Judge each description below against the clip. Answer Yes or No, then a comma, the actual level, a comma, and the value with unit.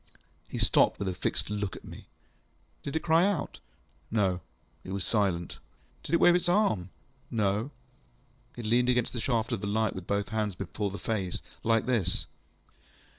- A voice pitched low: Yes, low, 110 Hz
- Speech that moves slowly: No, average, 175 wpm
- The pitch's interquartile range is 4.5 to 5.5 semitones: No, average, 4.1 semitones